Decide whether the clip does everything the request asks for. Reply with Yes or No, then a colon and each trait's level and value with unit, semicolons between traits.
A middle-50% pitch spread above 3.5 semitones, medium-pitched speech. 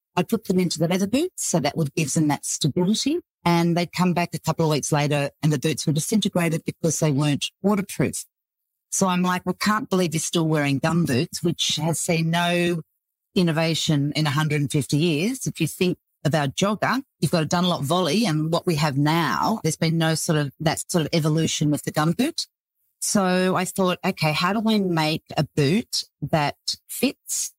No: average, 2.8 semitones; medium, 170 Hz